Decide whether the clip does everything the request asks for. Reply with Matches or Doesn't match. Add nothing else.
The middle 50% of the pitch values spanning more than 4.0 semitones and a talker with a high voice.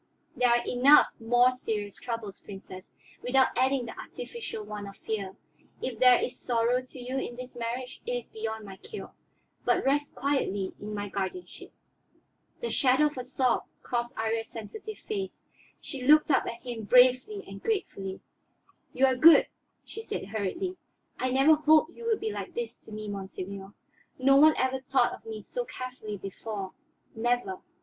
Matches